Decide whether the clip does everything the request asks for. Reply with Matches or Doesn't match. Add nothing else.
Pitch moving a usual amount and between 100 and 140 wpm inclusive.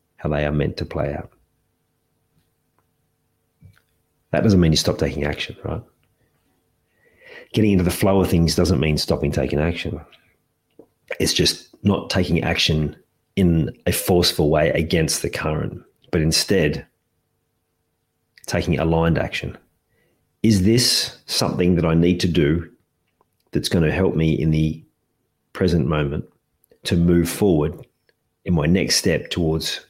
Doesn't match